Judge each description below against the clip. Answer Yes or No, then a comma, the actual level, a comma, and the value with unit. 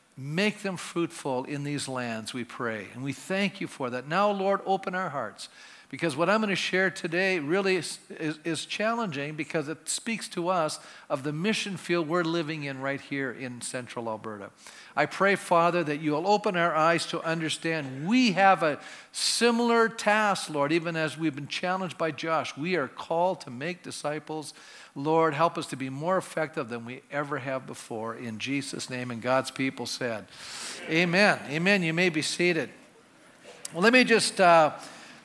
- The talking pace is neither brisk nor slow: Yes, average, 185 wpm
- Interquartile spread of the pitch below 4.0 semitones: No, average, 5.0 semitones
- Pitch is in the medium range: Yes, medium, 160 Hz